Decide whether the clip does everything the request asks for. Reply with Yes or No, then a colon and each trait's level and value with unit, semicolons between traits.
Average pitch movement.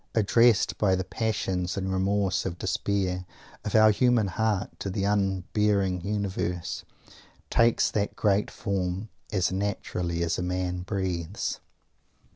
No: narrow, 2.2 semitones